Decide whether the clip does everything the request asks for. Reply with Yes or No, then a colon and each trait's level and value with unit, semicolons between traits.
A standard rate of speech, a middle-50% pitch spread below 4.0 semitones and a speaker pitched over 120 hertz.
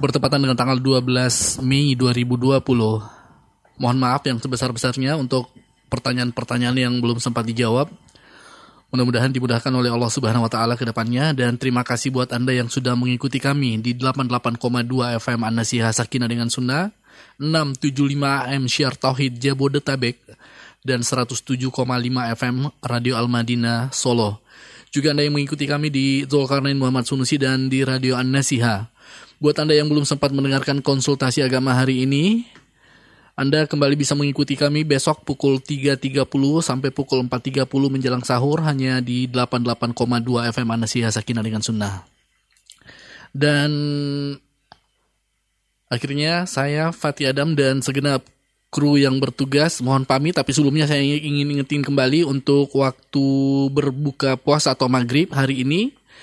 Yes: average, 130 wpm; narrow, 2.4 semitones; low, 130 Hz